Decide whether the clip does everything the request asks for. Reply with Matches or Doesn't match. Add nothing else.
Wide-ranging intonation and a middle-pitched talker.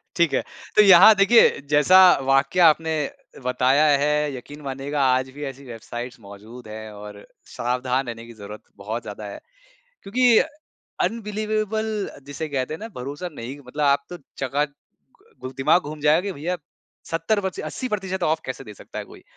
Matches